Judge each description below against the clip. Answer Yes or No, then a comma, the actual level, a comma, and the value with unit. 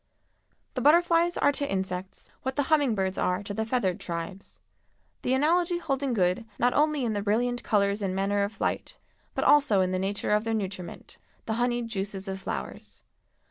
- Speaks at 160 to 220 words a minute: Yes, average, 180 wpm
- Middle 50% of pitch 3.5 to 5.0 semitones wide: No, wide, 5.6 semitones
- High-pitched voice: Yes, high, 215 Hz